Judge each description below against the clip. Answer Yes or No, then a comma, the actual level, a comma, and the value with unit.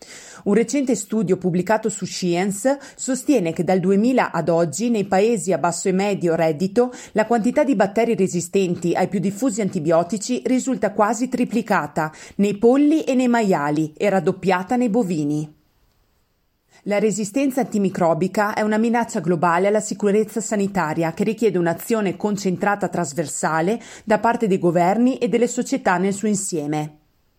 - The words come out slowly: No, average, 140 wpm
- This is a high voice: Yes, high, 205 Hz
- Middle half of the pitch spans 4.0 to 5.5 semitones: Yes, average, 4.7 semitones